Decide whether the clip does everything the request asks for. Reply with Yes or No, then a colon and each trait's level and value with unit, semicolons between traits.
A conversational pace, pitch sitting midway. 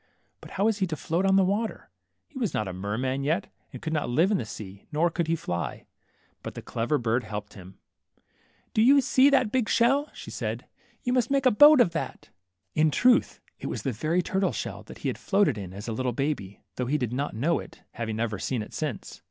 No: fast, 240 wpm; medium, 155 Hz